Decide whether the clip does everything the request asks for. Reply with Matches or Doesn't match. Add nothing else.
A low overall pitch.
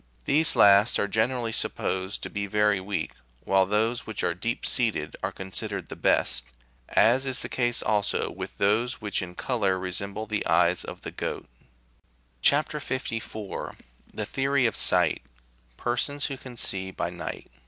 Matches